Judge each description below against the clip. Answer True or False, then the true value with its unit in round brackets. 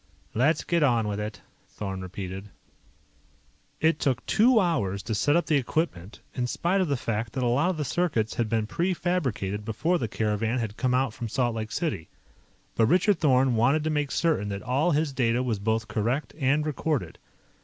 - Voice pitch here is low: True (125 Hz)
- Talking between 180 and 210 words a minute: True (190 wpm)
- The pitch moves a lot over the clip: True (6.2 semitones)